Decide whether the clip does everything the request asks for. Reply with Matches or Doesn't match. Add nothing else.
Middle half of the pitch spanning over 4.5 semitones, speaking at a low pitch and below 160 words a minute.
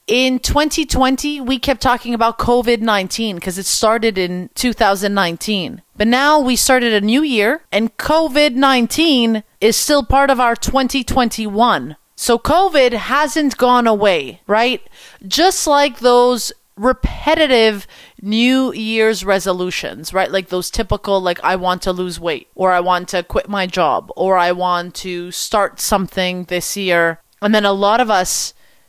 Doesn't match